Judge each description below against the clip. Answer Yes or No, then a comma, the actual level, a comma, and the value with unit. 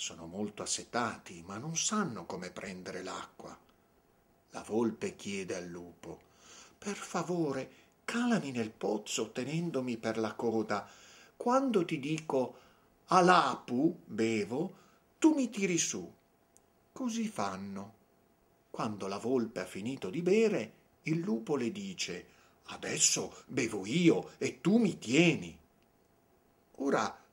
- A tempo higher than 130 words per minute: No, slow, 115 wpm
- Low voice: No, medium, 160 Hz